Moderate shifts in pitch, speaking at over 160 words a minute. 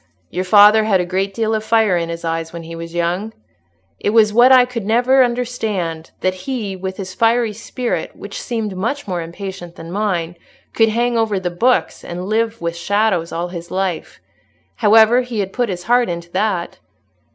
Yes: average, 4.5 semitones; average, 190 wpm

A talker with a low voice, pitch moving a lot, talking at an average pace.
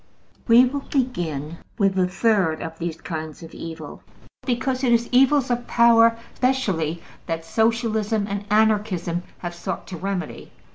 No: high, 205 Hz; wide, 5.9 semitones; average, 145 wpm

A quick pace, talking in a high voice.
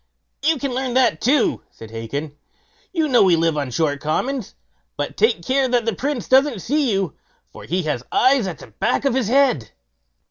No: average, 190 wpm; high, 235 Hz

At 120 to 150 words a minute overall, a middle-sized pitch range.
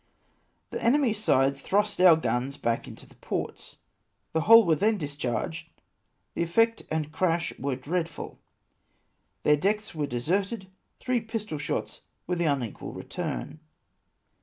No: average, 140 wpm; wide, 6.8 semitones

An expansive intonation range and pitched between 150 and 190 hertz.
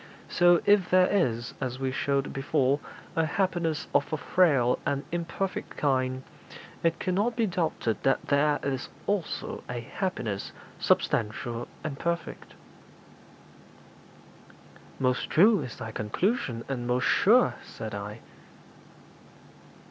No: wide, 6.3 semitones; medium, 140 Hz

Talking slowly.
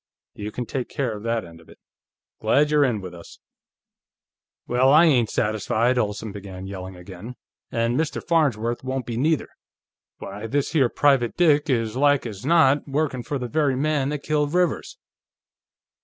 No: average, 170 wpm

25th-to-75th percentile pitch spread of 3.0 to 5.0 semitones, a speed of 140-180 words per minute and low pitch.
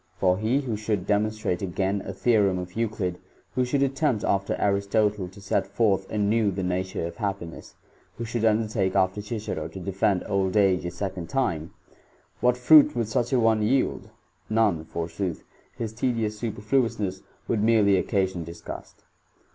Yes: average, 3.3 semitones; average, 170 wpm; low, 105 Hz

